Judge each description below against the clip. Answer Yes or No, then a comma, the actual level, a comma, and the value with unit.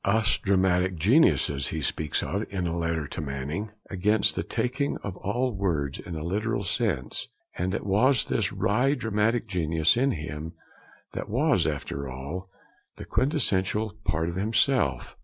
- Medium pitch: No, very low, 95 Hz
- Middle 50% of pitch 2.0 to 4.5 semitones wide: No, wide, 5.5 semitones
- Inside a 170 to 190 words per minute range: No, average, 155 wpm